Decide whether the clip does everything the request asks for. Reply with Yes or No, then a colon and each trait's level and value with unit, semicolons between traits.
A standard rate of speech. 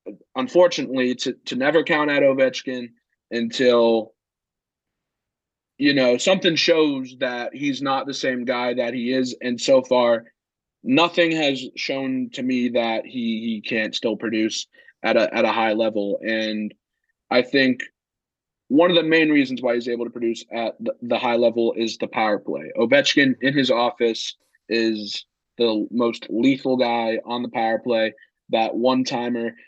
Yes: average, 160 wpm